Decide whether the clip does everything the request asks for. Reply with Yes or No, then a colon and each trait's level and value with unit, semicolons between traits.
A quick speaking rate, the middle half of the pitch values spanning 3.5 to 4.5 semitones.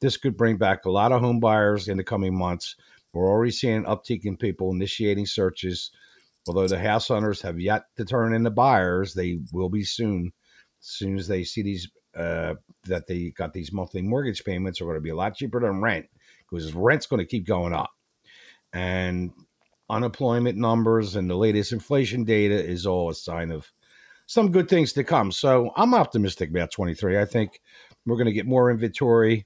No: average, 195 wpm; average, 4.2 semitones